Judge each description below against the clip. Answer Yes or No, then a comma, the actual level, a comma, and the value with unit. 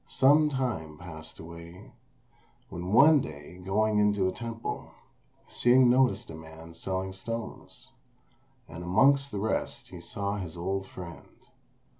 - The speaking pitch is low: Yes, very low, 95 Hz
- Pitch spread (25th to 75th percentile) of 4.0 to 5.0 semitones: No, wide, 5.4 semitones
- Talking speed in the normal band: No, slow, 130 wpm